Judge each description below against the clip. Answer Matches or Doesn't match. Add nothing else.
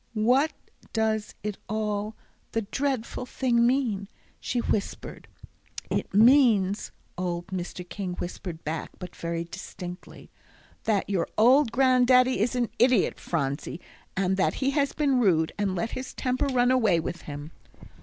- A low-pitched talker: Doesn't match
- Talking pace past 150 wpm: Doesn't match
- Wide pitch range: Matches